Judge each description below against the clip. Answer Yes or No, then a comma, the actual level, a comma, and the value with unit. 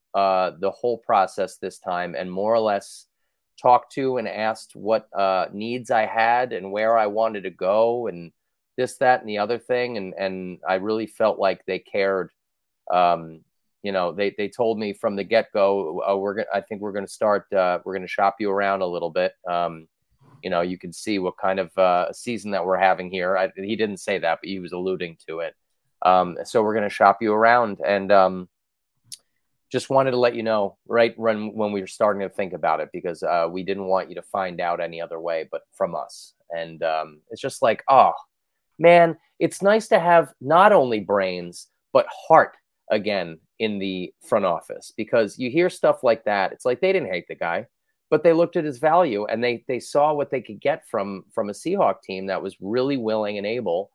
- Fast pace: Yes, fast, 215 wpm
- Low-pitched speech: Yes, low, 100 Hz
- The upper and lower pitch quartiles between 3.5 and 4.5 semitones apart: Yes, average, 3.8 semitones